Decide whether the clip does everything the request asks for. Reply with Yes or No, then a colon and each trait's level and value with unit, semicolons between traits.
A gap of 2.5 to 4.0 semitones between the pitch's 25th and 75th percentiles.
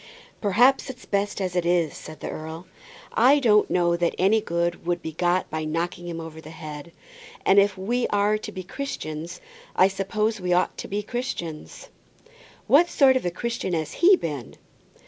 No: average, 4.4 semitones